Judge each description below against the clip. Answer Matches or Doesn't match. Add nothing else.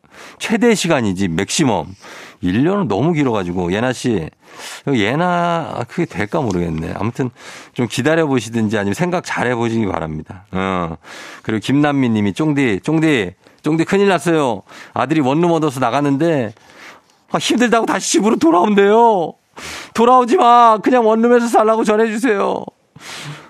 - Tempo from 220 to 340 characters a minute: Matches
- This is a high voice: Doesn't match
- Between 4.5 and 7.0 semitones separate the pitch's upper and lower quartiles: Doesn't match